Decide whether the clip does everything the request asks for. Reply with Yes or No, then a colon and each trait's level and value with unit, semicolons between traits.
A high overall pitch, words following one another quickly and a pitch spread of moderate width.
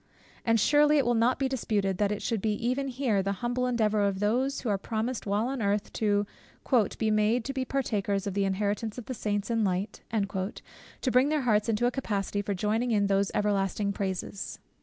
Yes: high, 215 Hz; fast, 210 wpm; average, 3.5 semitones